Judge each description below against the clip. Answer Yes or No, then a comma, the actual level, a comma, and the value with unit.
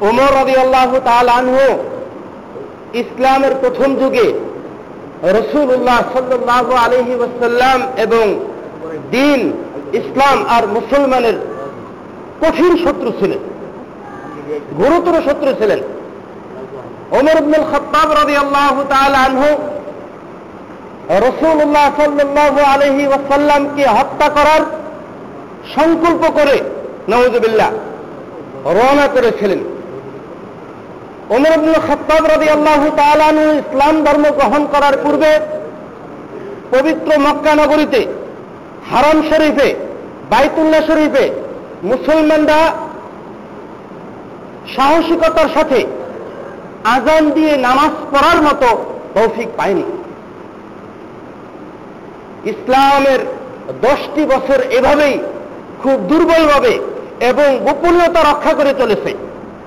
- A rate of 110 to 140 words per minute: No, average, 75 wpm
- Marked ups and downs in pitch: No, narrow, 2.6 semitones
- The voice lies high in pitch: Yes, very high, 295 Hz